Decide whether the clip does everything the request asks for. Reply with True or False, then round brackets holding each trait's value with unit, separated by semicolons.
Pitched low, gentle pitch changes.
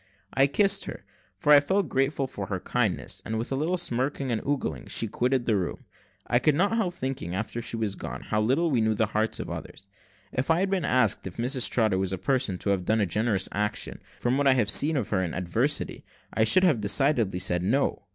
False (120 Hz; 5.3 semitones)